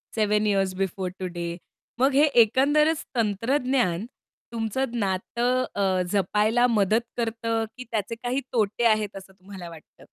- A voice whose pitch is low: No, high, 215 Hz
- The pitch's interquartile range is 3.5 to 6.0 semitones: Yes, average, 3.9 semitones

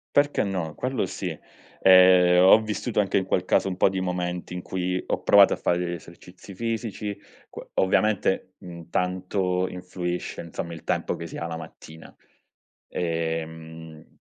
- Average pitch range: No, narrow, 2.0 semitones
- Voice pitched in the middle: No, very low, 90 Hz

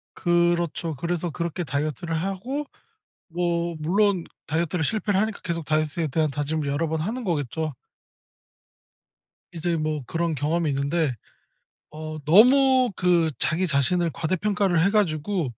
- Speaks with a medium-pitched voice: Yes, medium, 170 Hz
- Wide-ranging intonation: No, average, 3.0 semitones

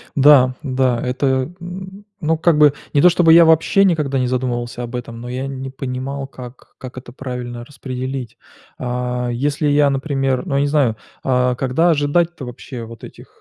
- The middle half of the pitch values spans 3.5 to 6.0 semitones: No, average, 2.9 semitones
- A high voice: No, low, 135 Hz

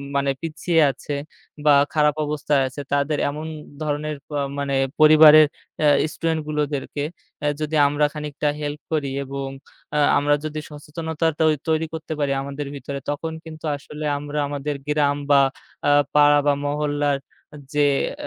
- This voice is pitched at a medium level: Yes, medium, 150 Hz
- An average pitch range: No, narrow, 1.1 semitones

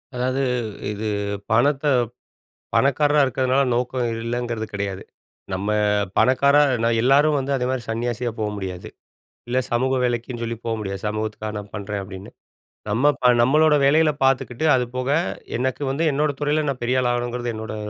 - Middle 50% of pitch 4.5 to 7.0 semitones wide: No, average, 3.6 semitones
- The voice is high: No, low, 125 Hz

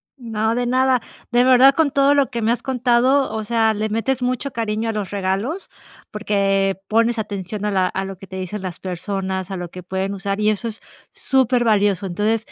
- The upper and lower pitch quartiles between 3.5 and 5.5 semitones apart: Yes, average, 3.9 semitones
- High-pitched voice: Yes, high, 215 Hz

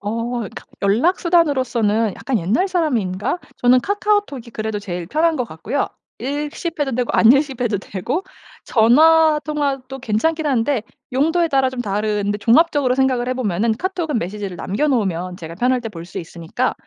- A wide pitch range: Yes, wide, 6.2 semitones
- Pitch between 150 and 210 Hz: No, very high, 250 Hz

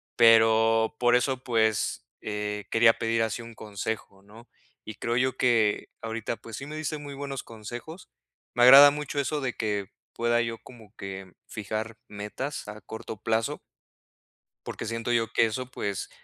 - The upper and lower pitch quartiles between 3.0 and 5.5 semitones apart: No, narrow, 2.4 semitones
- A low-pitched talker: Yes, low, 115 Hz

